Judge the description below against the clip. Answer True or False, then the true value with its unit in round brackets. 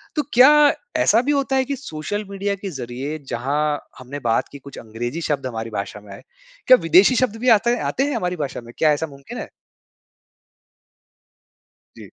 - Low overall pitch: False (160 Hz)